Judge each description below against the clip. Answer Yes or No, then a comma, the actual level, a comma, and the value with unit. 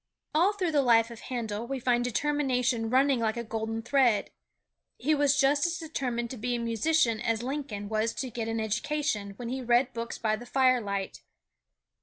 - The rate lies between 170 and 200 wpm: Yes, average, 185 wpm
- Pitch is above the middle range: Yes, high, 240 Hz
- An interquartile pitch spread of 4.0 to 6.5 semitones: No, average, 3.4 semitones